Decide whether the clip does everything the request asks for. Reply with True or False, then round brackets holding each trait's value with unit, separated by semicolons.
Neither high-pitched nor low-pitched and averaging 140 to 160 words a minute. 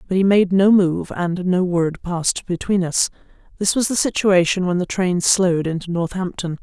False (180 Hz; 190 wpm)